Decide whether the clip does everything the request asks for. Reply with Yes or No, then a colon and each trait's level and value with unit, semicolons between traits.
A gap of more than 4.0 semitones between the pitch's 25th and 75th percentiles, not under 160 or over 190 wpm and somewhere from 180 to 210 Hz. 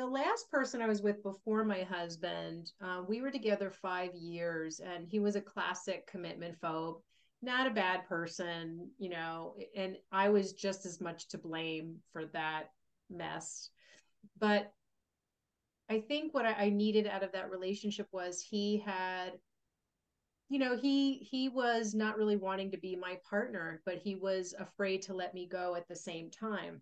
No: average, 3.0 semitones; average, 170 wpm; high, 190 Hz